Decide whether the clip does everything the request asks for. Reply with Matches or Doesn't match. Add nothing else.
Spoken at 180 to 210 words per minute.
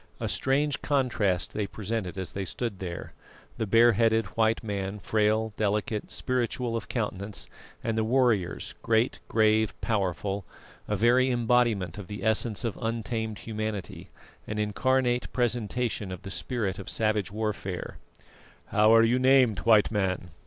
Doesn't match